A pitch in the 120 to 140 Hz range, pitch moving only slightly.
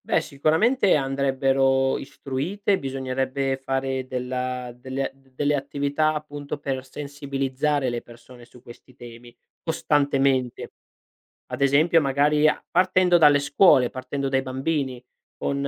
Yes: low, 135 Hz; narrow, 2.0 semitones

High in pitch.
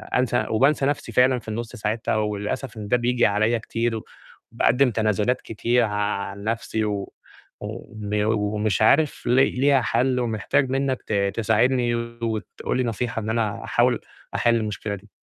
No: low, 115 Hz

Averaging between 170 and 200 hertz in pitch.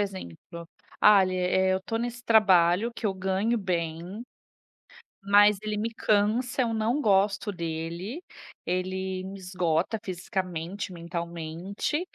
Yes: high, 190 Hz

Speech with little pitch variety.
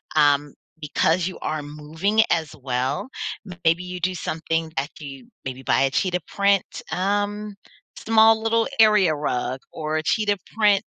No: wide, 5.6 semitones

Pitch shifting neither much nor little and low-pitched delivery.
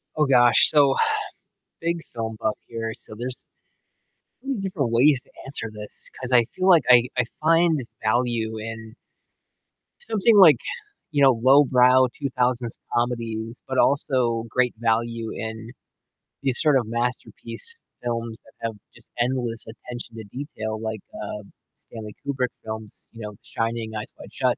Yes: average, 3.2 semitones; low, 120 Hz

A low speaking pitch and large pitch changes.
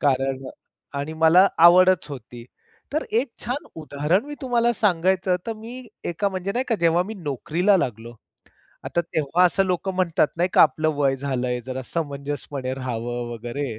No: medium, 165 Hz; wide, 5.8 semitones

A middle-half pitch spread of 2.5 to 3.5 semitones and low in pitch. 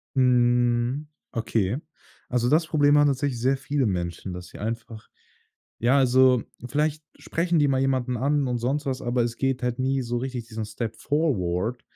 Yes: average, 2.9 semitones; low, 125 Hz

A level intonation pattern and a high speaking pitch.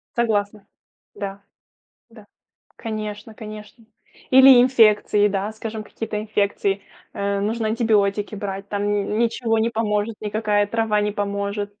Yes: narrow, 1.7 semitones; high, 210 Hz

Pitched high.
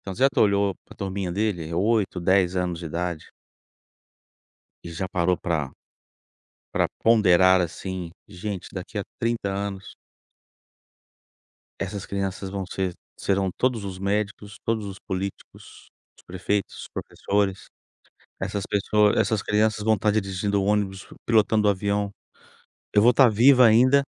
No: low, 100 Hz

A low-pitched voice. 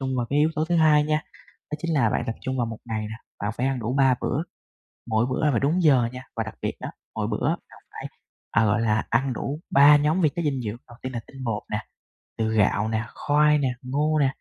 Yes: low, 130 Hz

